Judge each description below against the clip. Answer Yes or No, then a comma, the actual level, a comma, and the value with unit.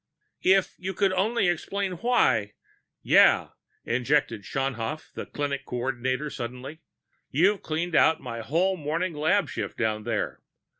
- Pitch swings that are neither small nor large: No, wide, 6.6 semitones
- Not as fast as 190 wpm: Yes, slow, 135 wpm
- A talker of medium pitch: Yes, medium, 150 Hz